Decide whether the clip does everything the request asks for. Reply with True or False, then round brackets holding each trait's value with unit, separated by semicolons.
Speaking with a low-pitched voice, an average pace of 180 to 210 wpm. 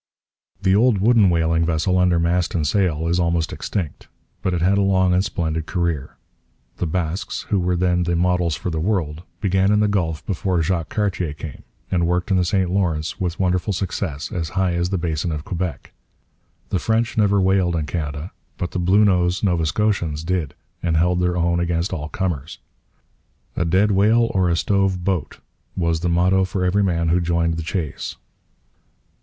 True (90 Hz; 185 wpm)